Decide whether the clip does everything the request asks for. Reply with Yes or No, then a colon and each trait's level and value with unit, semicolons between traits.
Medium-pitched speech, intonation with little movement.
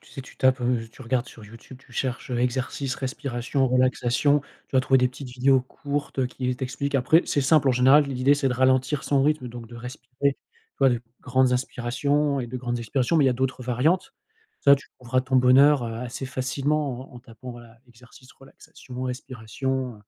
No: low, 130 Hz; narrow, 1.8 semitones